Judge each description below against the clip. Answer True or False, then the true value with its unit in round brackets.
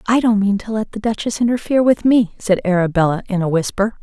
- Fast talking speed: True (225 wpm)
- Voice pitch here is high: True (210 Hz)